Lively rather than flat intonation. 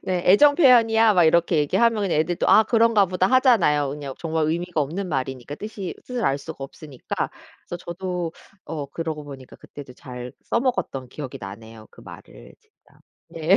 Yes: wide, 6.4 semitones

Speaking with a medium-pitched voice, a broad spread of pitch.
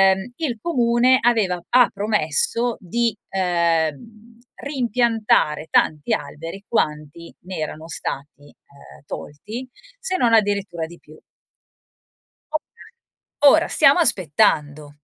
No: high, 200 Hz; wide, 7.4 semitones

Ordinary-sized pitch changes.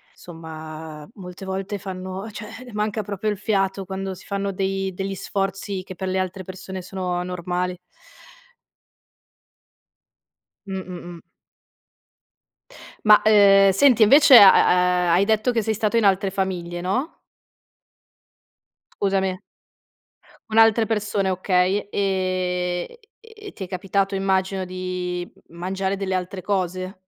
No: narrow, 1.8 semitones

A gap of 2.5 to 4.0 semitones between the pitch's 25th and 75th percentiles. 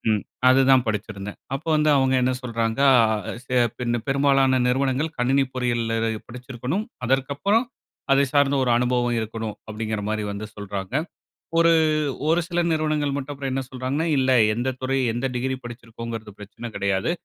Yes: average, 3.3 semitones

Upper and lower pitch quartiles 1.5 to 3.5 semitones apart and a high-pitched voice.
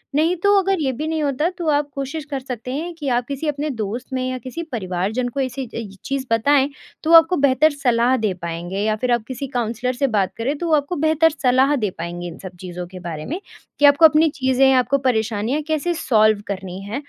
No: average, 5.2 semitones; very high, 260 Hz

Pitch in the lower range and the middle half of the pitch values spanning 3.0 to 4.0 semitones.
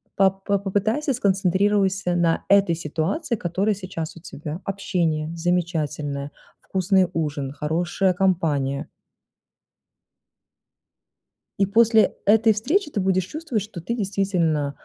No: medium, 185 Hz; average, 3.7 semitones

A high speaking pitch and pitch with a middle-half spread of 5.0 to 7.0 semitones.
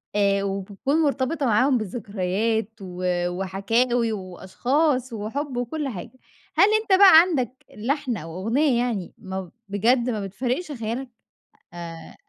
Yes: high, 230 Hz; average, 5.3 semitones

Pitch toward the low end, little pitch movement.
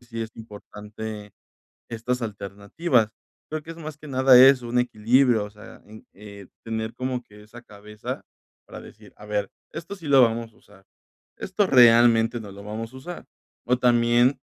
No: low, 115 Hz; average, 3.3 semitones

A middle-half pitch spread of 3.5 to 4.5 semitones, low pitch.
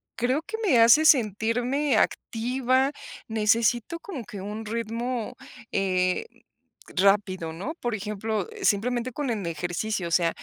No: average, 3.9 semitones; high, 225 Hz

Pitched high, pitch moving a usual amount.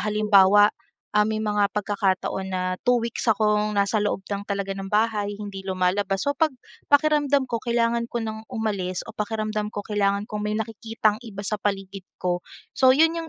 No: high, 210 Hz; narrow, 2.1 semitones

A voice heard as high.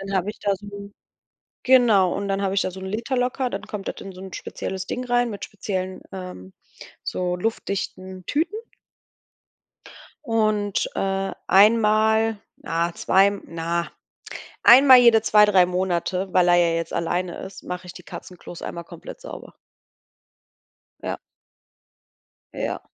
Yes: high, 195 Hz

